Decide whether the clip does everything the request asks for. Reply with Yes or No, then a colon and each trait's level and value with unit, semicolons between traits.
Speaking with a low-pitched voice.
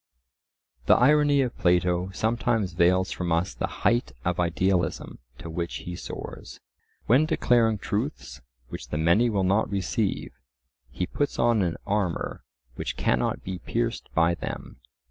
Yes: very low, 95 Hz